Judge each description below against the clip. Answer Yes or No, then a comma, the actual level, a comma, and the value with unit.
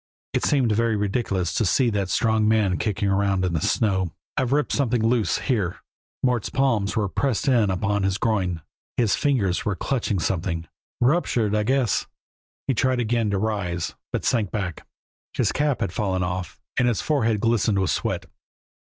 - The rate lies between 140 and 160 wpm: No, average, 170 wpm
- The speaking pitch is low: Yes, low, 105 Hz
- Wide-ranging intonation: No, average, 3.8 semitones